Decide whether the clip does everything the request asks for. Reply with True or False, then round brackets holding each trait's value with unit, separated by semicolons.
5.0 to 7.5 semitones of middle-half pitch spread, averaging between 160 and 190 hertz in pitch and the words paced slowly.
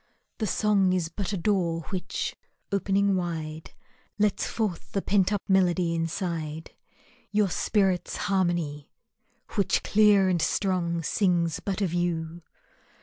False (2.9 semitones; 185 Hz; 125 wpm)